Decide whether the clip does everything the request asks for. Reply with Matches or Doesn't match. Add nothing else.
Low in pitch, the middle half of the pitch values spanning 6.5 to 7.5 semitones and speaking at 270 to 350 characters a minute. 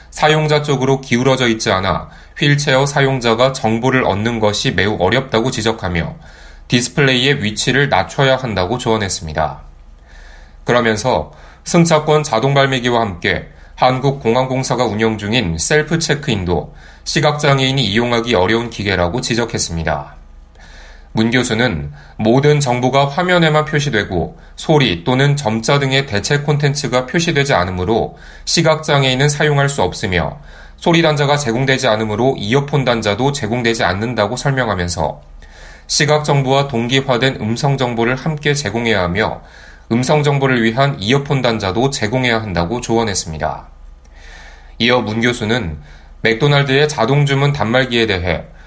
Matches